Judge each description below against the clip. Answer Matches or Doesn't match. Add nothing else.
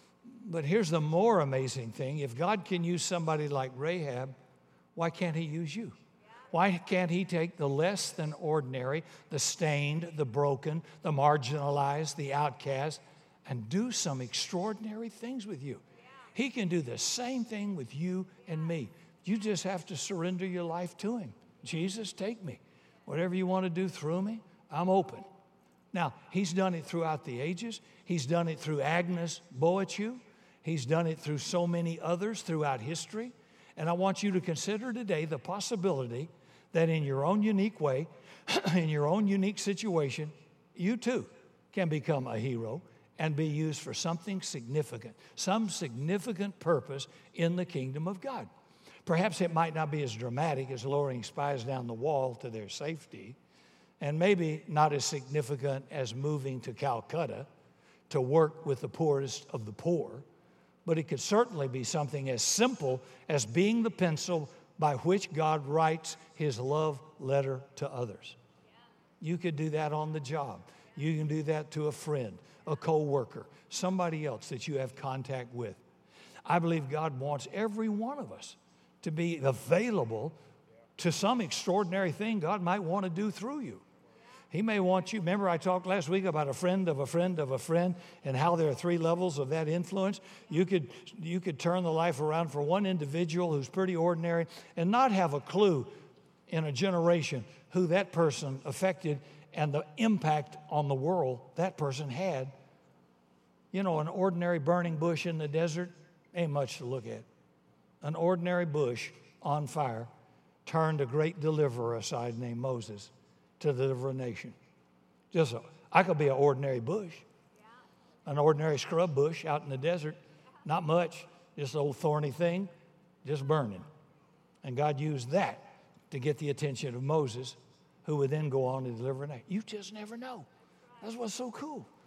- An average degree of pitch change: Matches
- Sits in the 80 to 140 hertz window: Doesn't match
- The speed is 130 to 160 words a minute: Doesn't match